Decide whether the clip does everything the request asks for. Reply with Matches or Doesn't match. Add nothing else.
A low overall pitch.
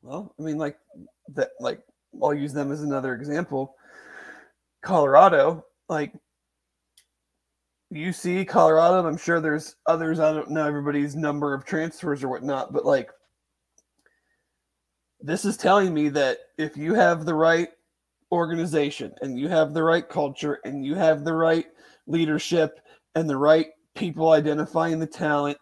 Doesn't match